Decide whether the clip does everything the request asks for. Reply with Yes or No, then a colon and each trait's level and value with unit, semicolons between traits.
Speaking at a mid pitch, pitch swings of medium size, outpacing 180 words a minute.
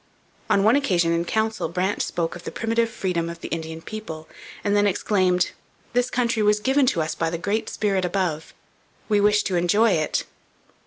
No: high, 195 Hz; average, 4.4 semitones; average, 190 wpm